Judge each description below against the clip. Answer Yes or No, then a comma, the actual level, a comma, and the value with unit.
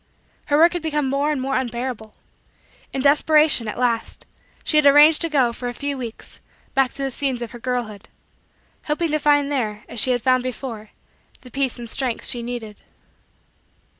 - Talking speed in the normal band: Yes, average, 185 wpm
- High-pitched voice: Yes, very high, 260 Hz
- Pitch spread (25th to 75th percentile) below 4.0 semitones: Yes, average, 3.3 semitones